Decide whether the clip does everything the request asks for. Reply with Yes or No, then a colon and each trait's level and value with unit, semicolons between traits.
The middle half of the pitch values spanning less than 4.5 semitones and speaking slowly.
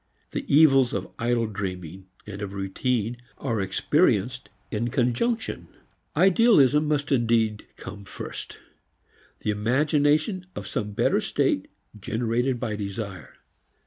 No: wide, 5.4 semitones; slow, 115 wpm